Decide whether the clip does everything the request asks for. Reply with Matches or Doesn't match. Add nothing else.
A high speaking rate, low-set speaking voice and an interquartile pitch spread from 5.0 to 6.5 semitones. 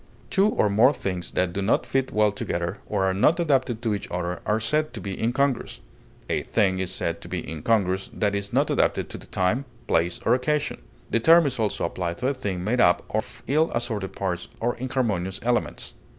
Matches